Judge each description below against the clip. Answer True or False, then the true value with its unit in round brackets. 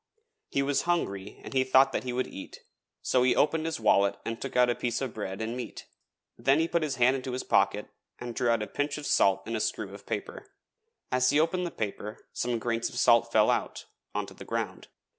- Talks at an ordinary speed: False (230 wpm)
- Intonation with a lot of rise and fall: False (3.2 semitones)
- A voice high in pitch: False (125 Hz)